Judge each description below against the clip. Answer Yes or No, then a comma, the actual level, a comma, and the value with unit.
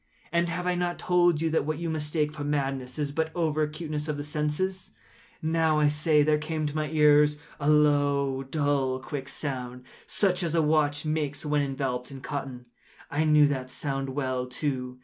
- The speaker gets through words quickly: No, average, 185 wpm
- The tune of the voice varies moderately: No, narrow, 2.2 semitones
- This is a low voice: No, medium, 150 Hz